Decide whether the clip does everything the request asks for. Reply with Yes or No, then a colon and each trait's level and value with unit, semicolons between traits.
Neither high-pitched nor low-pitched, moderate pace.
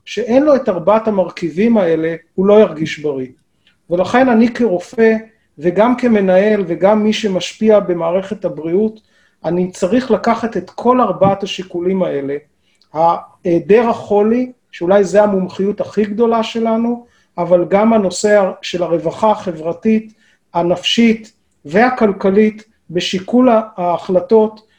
No: high, 205 Hz; average, 110 wpm